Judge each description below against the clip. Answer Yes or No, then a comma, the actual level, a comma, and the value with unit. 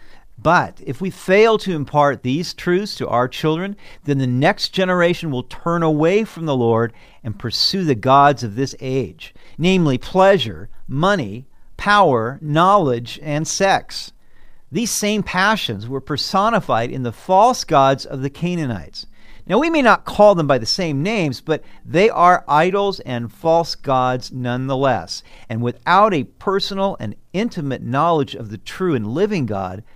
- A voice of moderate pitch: Yes, medium, 145 Hz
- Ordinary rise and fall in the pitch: No, wide, 7.0 semitones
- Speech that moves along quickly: No, average, 155 wpm